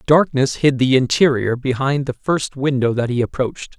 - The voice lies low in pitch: Yes, low, 130 Hz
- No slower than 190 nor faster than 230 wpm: No, average, 175 wpm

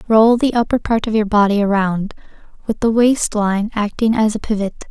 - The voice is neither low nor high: No, high, 215 Hz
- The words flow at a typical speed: Yes, average, 195 wpm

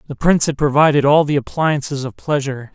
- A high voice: No, medium, 145 Hz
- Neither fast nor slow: Yes, average, 195 wpm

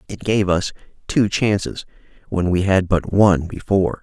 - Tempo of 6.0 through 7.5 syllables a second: No, 4.9 syllables/s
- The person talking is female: No, male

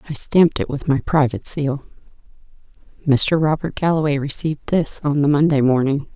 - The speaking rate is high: No, average, 155 wpm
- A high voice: No, medium, 145 Hz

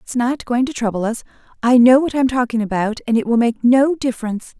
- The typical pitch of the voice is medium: No, high, 240 Hz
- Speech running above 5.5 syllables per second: Yes, 5.9 syllables/s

